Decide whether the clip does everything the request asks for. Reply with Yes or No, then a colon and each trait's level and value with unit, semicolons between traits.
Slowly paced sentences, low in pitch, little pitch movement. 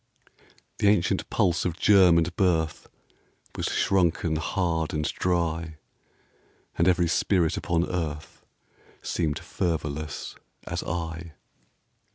Yes: slow, 105 wpm; very low, 85 Hz; narrow, 1.9 semitones